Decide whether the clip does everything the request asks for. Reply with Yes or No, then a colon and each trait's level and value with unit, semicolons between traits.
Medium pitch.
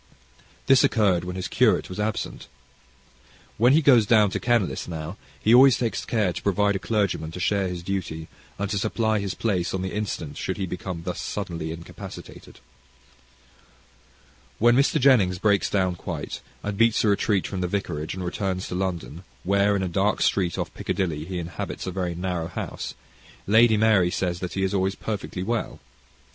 No: very low, 95 Hz